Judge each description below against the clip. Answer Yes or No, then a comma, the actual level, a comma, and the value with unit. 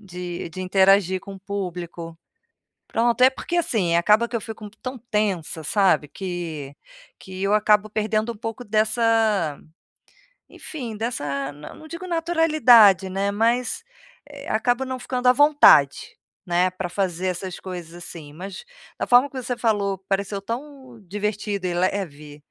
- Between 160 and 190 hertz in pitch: No, high, 205 Hz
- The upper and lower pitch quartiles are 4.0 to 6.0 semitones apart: Yes, average, 4.9 semitones